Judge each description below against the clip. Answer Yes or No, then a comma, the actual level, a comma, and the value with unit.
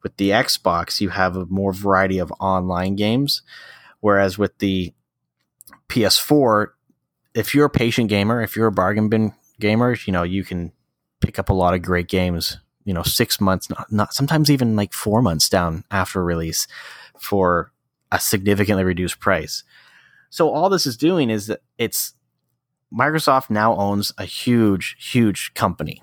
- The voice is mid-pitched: No, low, 100 Hz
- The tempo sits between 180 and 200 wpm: No, average, 165 wpm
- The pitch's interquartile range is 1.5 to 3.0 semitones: No, average, 3.4 semitones